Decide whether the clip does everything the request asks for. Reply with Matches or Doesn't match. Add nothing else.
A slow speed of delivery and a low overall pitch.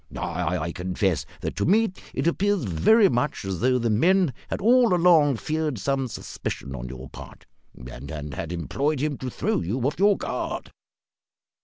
Doesn't match